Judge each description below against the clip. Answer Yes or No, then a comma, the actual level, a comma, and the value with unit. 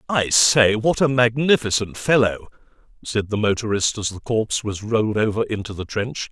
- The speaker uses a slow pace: No, average, 170 wpm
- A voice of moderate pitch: No, low, 110 Hz